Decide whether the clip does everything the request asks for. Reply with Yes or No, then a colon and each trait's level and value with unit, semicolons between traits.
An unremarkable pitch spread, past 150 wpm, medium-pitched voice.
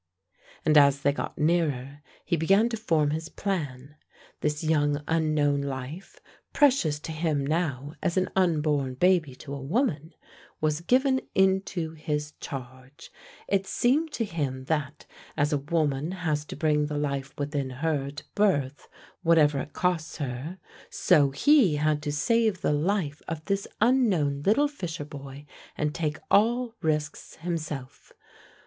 No: average, 3.9 semitones; average, 145 wpm; medium, 155 Hz